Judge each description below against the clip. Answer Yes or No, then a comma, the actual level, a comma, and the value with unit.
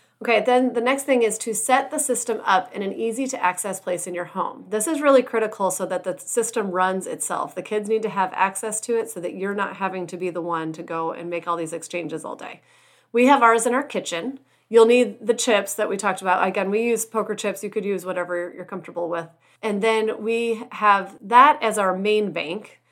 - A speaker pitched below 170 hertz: No, high, 210 Hz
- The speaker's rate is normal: No, fast, 240 wpm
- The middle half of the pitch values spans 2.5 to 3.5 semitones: No, average, 4.0 semitones